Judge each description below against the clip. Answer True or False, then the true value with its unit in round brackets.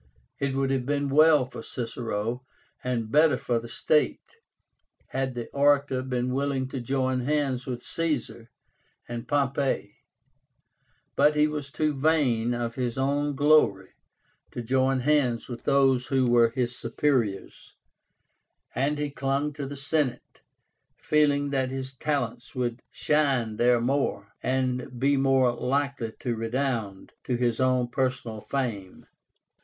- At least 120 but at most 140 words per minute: True (135 wpm)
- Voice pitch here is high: False (130 Hz)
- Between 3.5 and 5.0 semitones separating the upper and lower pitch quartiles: False (2.8 semitones)